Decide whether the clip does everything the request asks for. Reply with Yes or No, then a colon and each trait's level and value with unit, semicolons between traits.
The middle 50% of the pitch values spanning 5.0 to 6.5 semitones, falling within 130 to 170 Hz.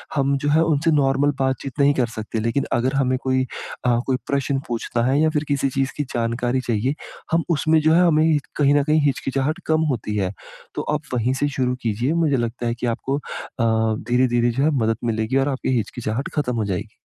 No: average, 3.3 semitones; low, 135 Hz